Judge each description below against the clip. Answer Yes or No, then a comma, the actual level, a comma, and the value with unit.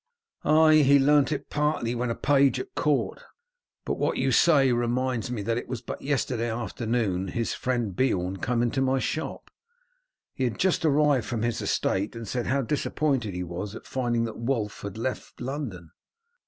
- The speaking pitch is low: Yes, low, 120 Hz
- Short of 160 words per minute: No, average, 180 wpm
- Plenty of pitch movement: No, average, 3.4 semitones